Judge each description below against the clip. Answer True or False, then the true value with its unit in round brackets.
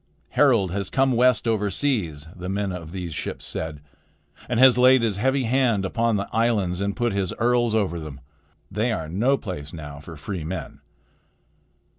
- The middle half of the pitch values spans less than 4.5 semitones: False (5.4 semitones)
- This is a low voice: True (100 Hz)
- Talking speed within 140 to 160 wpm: False (175 wpm)